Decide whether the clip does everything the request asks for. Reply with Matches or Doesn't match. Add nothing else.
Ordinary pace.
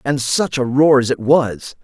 Doesn't match